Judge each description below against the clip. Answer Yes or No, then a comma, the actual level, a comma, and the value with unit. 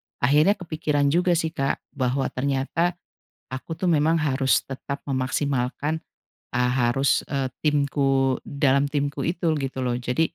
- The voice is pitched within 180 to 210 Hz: No, medium, 140 Hz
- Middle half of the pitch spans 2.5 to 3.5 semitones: Yes, average, 2.8 semitones